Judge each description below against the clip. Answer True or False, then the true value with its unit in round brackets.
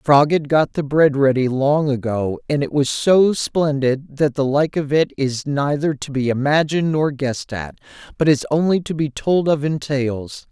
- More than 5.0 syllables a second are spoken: False (4.6 syllables/s)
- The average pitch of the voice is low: False (145 Hz)